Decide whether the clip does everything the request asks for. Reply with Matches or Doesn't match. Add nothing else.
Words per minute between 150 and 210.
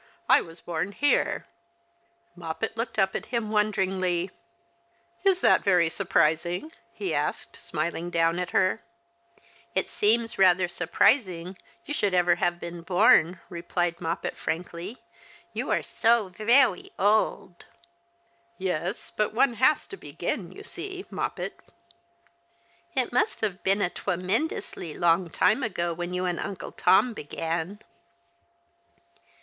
Doesn't match